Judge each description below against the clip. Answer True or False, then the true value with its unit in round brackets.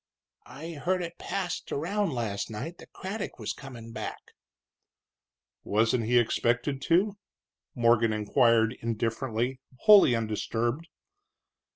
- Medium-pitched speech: False (125 Hz)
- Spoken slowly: True (110 wpm)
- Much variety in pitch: True (6.7 semitones)